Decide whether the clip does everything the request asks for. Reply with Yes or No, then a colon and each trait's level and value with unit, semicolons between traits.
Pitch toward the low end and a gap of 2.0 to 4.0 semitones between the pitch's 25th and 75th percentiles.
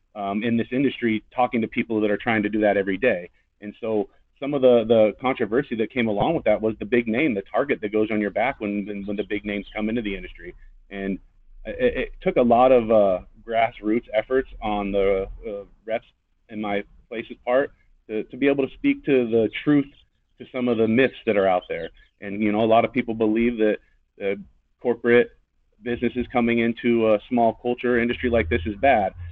Yes: low, 110 Hz; average, 2.7 semitones